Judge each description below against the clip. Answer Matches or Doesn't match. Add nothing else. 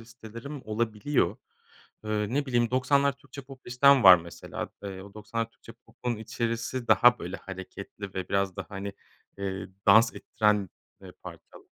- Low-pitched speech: Matches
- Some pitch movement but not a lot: Matches